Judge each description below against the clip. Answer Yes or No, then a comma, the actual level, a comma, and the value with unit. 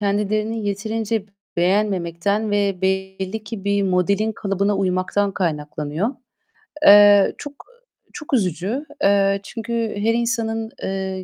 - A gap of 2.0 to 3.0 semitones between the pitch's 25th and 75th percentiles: Yes, narrow, 2.6 semitones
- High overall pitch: Yes, high, 200 Hz